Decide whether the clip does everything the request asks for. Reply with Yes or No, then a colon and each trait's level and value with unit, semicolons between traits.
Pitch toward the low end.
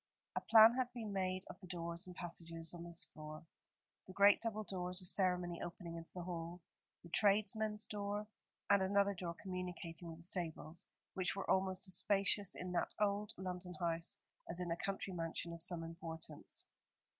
No: medium, 180 Hz